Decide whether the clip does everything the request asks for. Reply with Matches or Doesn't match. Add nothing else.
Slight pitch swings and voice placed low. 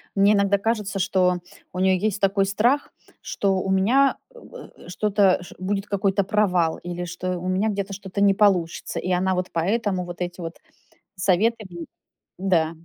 Doesn't match